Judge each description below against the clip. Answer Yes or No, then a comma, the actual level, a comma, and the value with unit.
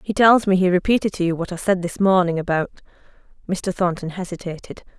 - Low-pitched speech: No, medium, 185 Hz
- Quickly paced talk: No, average, 190 wpm